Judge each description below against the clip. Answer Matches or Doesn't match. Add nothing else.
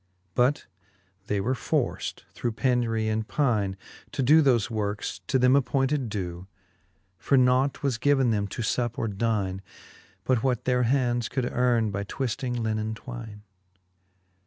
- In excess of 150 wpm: Doesn't match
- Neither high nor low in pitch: Doesn't match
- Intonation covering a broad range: Doesn't match